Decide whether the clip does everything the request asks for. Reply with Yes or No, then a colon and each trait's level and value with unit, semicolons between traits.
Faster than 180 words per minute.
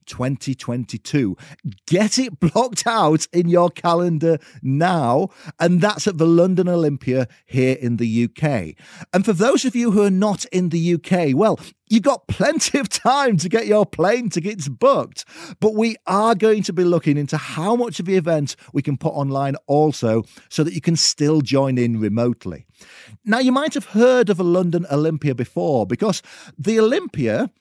No: average, 175 wpm